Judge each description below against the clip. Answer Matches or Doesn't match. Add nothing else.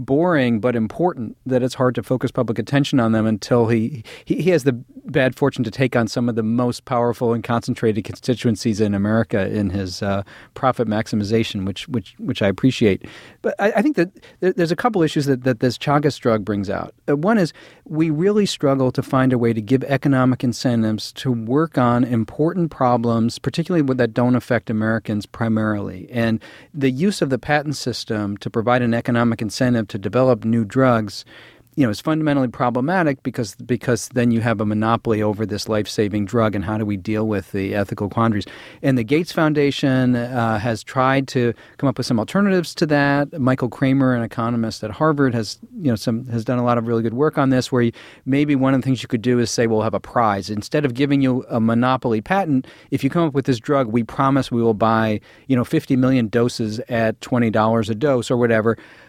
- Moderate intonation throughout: Matches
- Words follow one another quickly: Matches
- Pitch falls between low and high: Doesn't match